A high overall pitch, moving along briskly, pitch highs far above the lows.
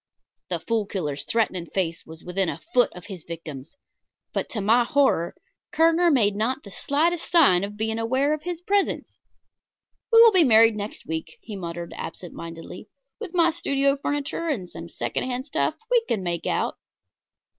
No: high, 220 Hz; average, 175 wpm; wide, 8.6 semitones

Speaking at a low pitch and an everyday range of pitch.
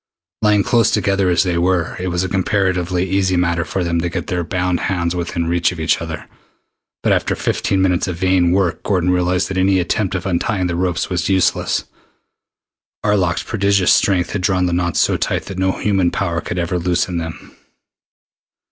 No: very low, 90 Hz; narrow, 1.6 semitones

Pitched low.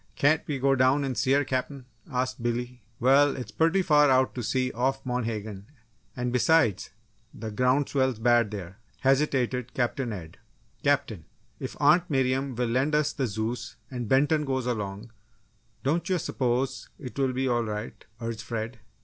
Yes: low, 125 Hz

